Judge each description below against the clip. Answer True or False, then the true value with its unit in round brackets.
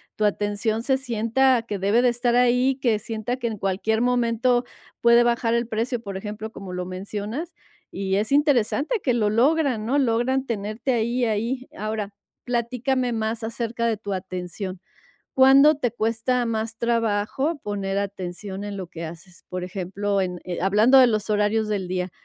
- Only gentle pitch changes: False (3.2 semitones)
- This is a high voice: True (225 Hz)